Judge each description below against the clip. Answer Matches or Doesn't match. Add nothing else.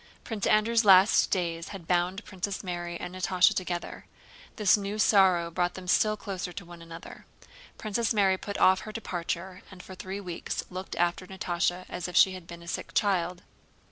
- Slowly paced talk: Doesn't match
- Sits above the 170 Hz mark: Matches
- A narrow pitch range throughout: Matches